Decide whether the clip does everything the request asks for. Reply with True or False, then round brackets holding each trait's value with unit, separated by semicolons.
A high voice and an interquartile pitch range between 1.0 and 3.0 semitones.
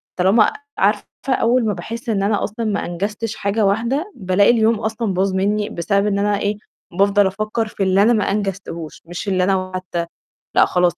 True (205 Hz; 2.4 semitones)